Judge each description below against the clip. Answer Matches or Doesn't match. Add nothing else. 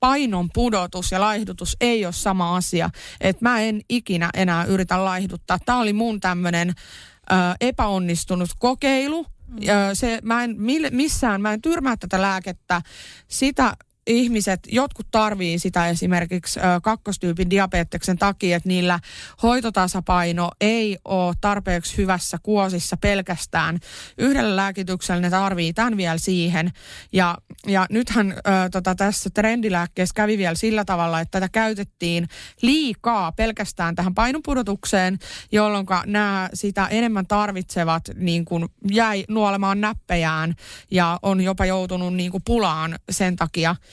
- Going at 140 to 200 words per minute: Doesn't match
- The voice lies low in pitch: Doesn't match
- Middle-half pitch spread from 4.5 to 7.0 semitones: Doesn't match